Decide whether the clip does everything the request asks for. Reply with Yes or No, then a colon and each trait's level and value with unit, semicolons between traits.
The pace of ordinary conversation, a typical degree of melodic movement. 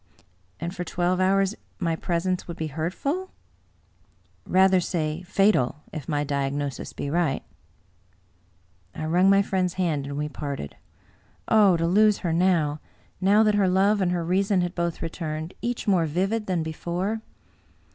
Yes: average, 160 wpm; average, 3.6 semitones